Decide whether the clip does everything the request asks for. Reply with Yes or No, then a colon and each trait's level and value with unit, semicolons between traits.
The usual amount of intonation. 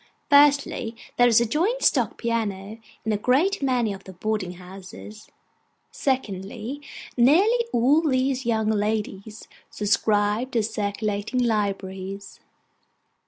Yes: average, 4.1 semitones